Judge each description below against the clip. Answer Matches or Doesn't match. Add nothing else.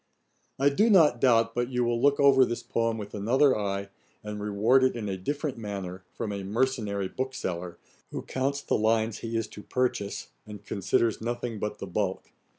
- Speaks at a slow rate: Doesn't match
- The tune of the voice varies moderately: Matches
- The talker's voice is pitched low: Matches